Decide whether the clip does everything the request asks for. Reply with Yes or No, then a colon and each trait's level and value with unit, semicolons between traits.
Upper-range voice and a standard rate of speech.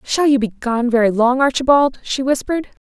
Yes: very high, 255 Hz; average, 190 wpm